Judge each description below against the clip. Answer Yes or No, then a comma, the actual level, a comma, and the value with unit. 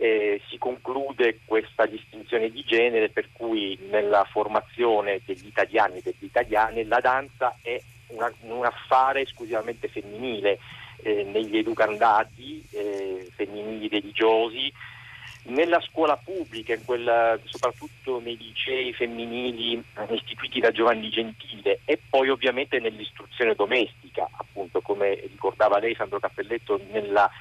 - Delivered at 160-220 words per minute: No, average, 120 wpm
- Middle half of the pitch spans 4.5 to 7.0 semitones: No, average, 4.0 semitones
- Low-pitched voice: Yes, low, 120 Hz